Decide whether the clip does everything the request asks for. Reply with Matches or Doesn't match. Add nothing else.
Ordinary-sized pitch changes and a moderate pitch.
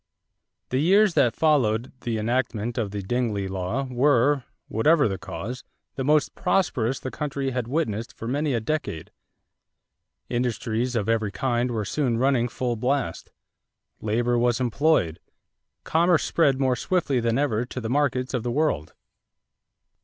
Doesn't match